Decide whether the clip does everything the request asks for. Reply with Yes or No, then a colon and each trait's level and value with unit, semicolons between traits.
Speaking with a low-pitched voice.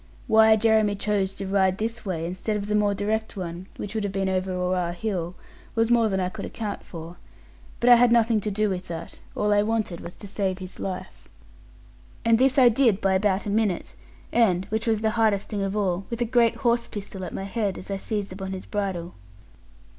No: high, 205 Hz